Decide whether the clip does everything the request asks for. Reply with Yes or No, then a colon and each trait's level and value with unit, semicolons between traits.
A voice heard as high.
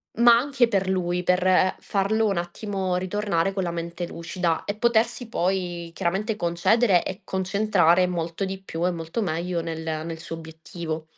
No: medium, 180 Hz